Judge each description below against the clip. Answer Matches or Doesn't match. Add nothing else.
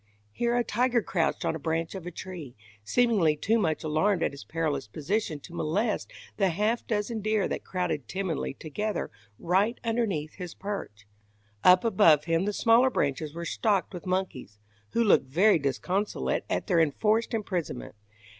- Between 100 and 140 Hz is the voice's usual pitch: Doesn't match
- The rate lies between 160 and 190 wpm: Matches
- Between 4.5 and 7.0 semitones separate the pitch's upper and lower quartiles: Matches